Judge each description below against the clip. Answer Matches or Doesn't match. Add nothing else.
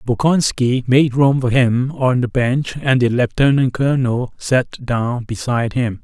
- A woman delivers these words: Doesn't match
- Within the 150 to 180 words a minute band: Matches